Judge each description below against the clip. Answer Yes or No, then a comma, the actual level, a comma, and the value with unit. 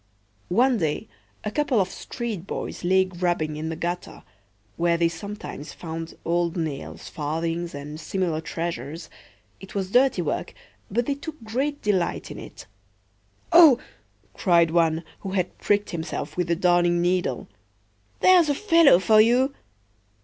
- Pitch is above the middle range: No, medium, 180 Hz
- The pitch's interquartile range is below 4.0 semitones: No, average, 4.8 semitones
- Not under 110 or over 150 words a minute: Yes, average, 140 wpm